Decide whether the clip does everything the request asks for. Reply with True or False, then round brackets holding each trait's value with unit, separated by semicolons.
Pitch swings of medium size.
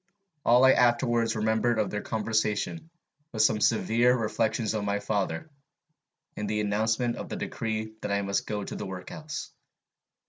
False (2.3 semitones)